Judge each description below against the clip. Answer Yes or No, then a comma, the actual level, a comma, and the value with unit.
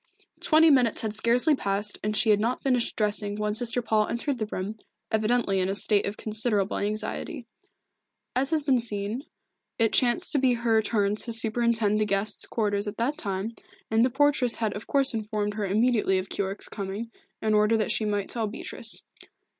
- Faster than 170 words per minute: Yes, average, 185 wpm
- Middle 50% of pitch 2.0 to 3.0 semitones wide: Yes, narrow, 2.5 semitones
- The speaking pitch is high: Yes, high, 220 Hz